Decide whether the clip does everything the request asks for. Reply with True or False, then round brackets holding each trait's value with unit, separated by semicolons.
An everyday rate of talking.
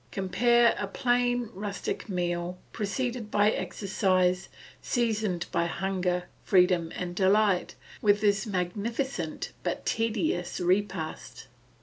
False (100 wpm)